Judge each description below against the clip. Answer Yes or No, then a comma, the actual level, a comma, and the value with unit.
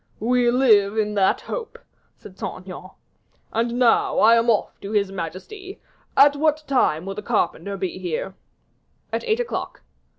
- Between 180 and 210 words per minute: No, average, 160 wpm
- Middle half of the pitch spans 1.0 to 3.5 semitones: No, average, 5.0 semitones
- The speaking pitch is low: No, high, 220 Hz